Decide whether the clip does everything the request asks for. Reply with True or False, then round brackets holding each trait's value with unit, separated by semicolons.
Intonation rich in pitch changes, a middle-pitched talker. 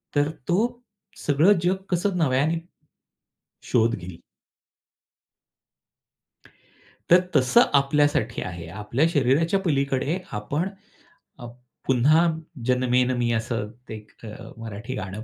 False (6.0 semitones; 130 Hz)